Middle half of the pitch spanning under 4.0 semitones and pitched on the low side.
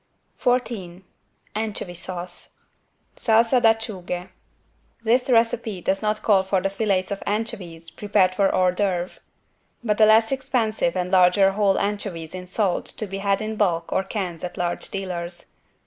No: average, 3.2 semitones; high, 195 Hz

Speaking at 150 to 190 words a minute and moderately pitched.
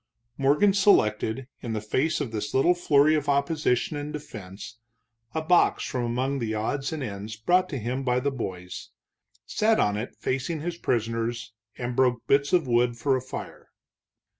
No: average, 165 wpm; low, 130 Hz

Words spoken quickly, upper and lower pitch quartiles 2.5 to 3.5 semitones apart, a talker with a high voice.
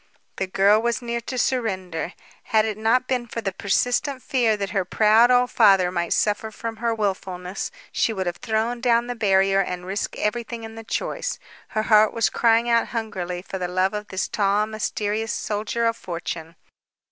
No: average, 185 wpm; average, 3.2 semitones; high, 215 Hz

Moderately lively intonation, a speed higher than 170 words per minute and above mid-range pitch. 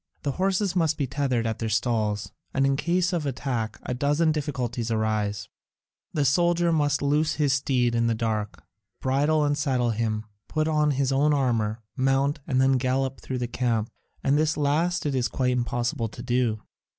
No: average, 3.9 semitones; average, 180 wpm; low, 135 Hz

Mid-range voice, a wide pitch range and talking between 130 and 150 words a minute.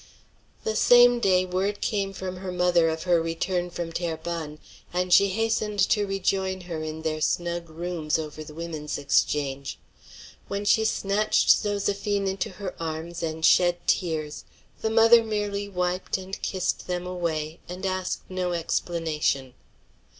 No: medium, 180 Hz; average, 3.2 semitones; average, 145 wpm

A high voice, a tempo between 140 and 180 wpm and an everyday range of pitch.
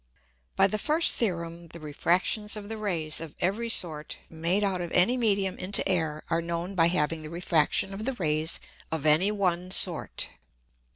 No: medium, 175 Hz; average, 175 wpm; average, 3.5 semitones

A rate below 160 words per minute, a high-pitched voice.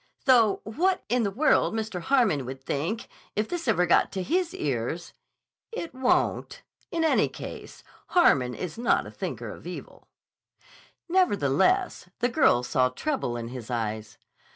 Yes: average, 150 wpm; high, 210 Hz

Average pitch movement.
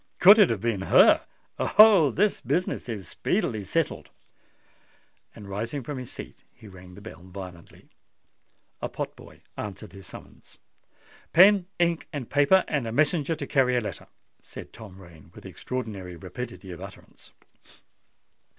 No: wide, 8.1 semitones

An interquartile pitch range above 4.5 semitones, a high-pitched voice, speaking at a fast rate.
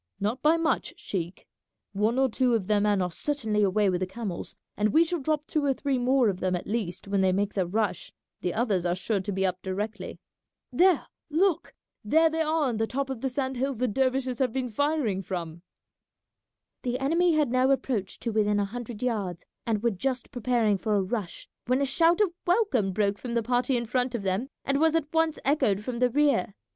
Yes: average, 5.2 semitones; high, 235 Hz; fast, 220 wpm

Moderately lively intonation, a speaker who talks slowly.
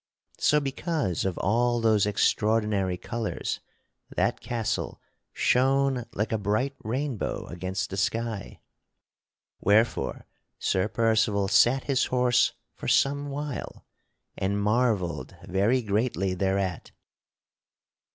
Yes: average, 4.2 semitones; slow, 105 wpm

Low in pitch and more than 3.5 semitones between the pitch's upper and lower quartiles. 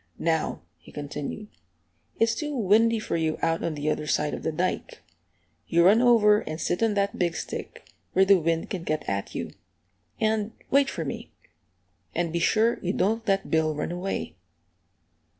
No: medium, 185 Hz; average, 5.2 semitones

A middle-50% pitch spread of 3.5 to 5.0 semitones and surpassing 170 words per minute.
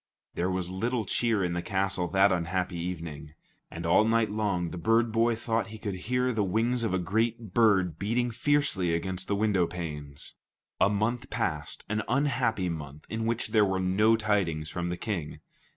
Yes: average, 4.3 semitones; average, 185 wpm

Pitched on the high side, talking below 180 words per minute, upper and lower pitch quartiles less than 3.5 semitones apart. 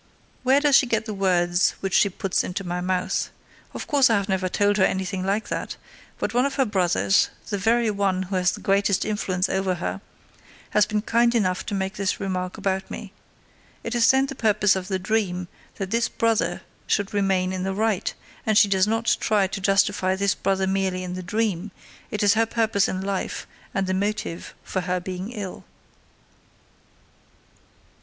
No: high, 195 Hz; average, 190 wpm; narrow, 2.5 semitones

